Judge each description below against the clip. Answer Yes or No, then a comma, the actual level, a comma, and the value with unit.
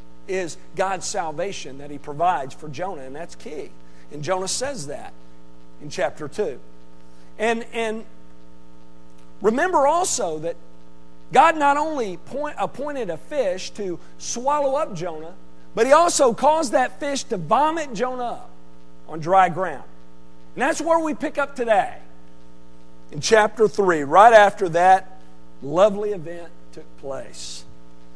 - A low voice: No, medium, 175 Hz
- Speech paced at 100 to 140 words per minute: Yes, slow, 135 wpm